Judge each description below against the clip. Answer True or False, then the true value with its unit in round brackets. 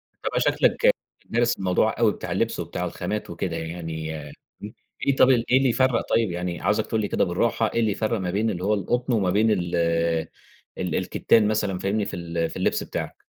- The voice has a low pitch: True (105 Hz)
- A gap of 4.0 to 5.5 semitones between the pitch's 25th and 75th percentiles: True (4.3 semitones)